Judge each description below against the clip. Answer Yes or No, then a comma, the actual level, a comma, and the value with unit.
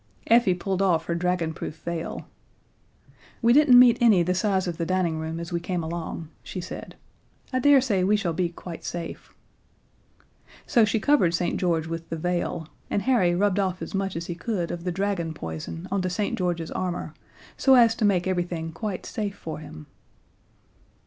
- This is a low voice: No, medium, 180 Hz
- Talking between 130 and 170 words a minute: No, average, 180 wpm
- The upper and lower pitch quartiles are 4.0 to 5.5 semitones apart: No, average, 3.2 semitones